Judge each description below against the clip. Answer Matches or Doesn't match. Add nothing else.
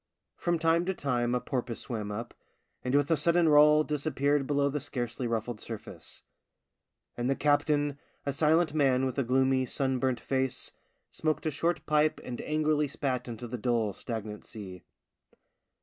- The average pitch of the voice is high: Doesn't match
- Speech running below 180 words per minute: Matches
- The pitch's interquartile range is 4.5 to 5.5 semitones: Doesn't match